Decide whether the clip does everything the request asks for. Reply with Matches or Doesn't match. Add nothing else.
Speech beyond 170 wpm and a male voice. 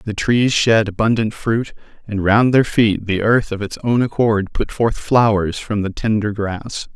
Matches